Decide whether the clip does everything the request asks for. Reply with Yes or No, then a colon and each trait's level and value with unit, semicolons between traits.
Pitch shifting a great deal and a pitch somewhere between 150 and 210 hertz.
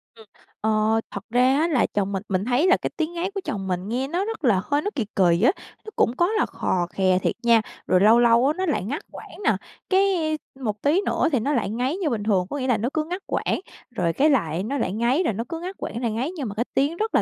No: wide, 7.2 semitones; high, 245 Hz